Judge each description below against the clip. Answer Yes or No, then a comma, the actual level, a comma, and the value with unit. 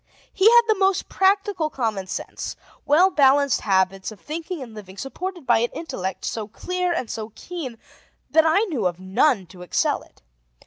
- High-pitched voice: Yes, very high, 275 Hz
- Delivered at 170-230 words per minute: Yes, average, 175 wpm